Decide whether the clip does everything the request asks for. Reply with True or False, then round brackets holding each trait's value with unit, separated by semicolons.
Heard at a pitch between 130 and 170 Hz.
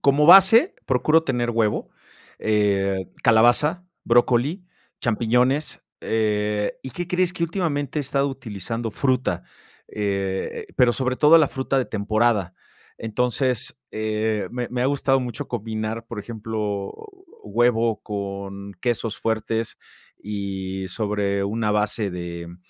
False (115 Hz)